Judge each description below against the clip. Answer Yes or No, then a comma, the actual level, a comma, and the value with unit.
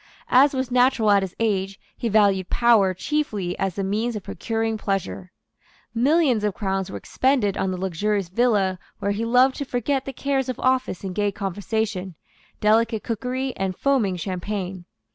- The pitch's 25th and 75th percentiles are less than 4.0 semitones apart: No, average, 4.5 semitones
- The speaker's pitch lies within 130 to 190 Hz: No, high, 210 Hz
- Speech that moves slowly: No, average, 165 wpm